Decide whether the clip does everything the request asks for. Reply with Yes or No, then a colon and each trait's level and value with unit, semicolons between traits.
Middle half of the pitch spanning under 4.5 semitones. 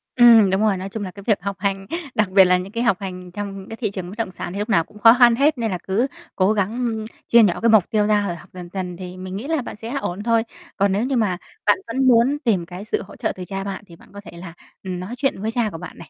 Yes: average, 3.4 semitones